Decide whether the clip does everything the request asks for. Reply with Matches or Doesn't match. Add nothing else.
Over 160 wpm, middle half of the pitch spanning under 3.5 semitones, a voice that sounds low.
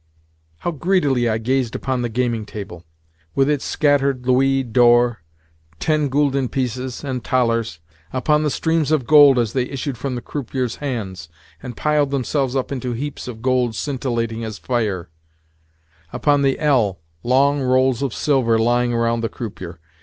Doesn't match